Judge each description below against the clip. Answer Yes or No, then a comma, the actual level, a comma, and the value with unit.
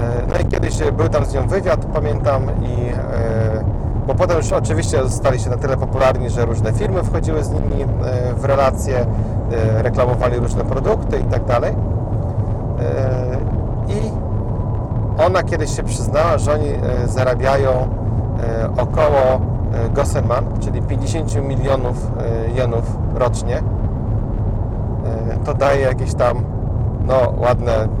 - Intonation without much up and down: Yes, narrow, 2.1 semitones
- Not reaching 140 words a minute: Yes, slow, 110 wpm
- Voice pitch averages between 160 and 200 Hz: No, low, 110 Hz